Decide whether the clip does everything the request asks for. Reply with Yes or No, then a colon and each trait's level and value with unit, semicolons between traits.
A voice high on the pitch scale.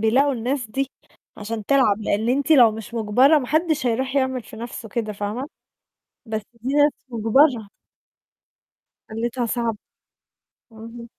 Yes: high, 235 Hz